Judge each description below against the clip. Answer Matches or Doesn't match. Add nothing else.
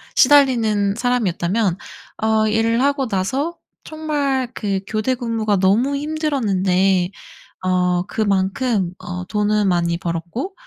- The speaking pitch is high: Matches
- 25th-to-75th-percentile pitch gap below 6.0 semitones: Matches